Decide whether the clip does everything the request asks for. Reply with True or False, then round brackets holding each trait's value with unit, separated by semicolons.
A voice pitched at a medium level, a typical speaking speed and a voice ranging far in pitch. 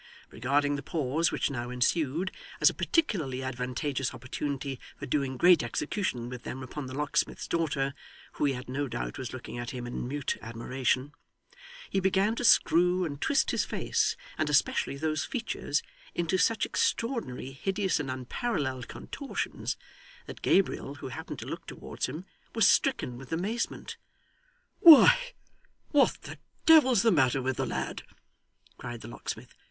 True (145 Hz; 155 wpm; 6.0 semitones)